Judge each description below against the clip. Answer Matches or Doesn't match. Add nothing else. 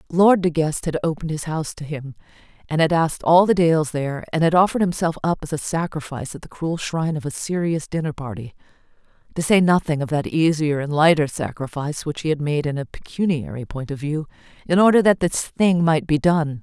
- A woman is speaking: Matches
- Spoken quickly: Matches